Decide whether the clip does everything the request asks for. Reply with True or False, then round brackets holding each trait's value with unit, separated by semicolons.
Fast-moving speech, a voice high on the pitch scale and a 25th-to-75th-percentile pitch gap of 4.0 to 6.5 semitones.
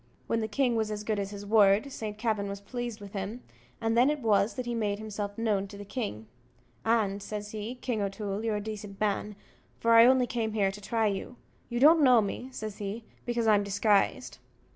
False (215 wpm; 215 Hz; 2.4 semitones)